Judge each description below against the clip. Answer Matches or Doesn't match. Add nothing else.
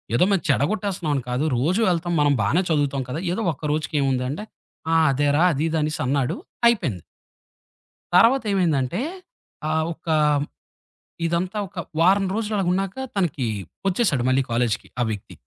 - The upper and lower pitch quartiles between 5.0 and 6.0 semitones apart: Matches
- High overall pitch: Doesn't match